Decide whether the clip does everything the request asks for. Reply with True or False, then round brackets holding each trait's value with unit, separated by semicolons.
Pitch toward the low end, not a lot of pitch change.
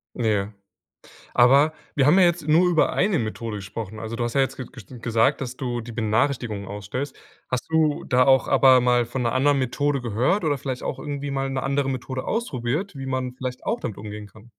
False (130 Hz; 3.5 semitones)